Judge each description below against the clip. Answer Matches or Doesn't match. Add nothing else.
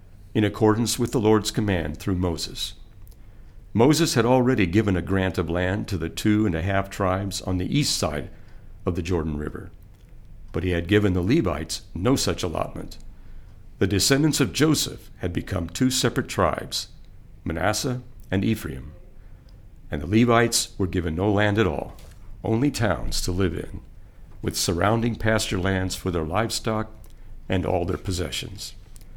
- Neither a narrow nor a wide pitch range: Matches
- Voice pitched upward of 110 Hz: Doesn't match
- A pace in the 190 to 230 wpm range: Doesn't match